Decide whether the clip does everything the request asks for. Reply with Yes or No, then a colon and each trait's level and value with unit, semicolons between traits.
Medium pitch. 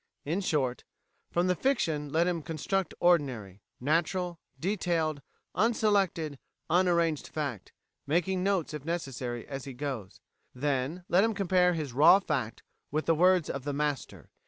Yes: medium, 160 Hz